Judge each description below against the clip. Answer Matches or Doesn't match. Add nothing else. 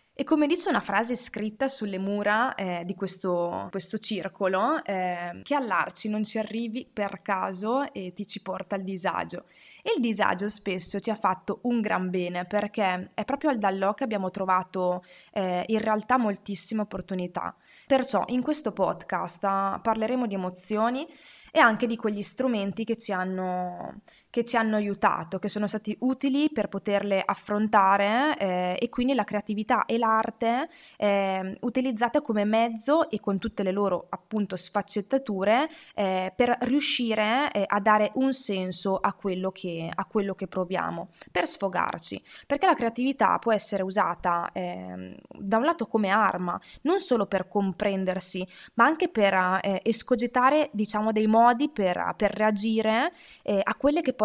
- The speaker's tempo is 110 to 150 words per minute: Doesn't match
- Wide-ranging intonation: Doesn't match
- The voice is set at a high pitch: Matches